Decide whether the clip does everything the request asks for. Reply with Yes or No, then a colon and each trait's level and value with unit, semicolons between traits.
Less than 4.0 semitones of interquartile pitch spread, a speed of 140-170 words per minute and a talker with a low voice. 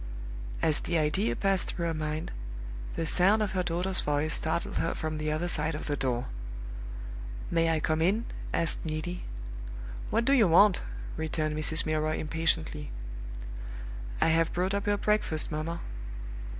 No: average, 2.7 semitones; average, 155 wpm; medium, 160 Hz